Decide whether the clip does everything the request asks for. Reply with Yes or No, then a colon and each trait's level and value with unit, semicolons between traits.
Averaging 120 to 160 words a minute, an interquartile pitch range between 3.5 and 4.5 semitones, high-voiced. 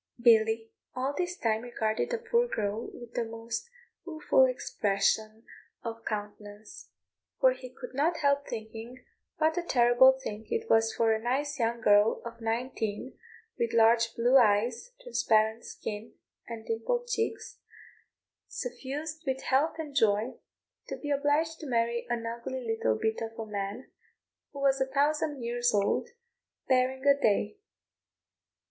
Yes: average, 145 wpm; average, 4.0 semitones; high, 240 Hz